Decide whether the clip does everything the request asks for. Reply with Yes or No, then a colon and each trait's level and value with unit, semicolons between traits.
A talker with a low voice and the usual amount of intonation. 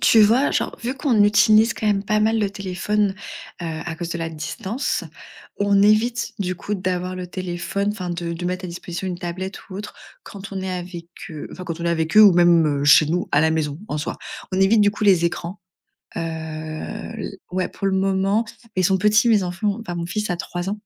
No: medium, 185 Hz; average, 3.3 semitones